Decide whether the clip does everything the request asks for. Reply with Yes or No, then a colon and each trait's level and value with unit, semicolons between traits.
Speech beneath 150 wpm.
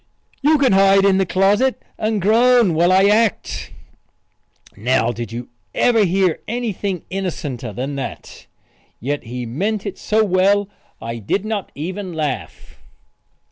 Yes: average, 140 wpm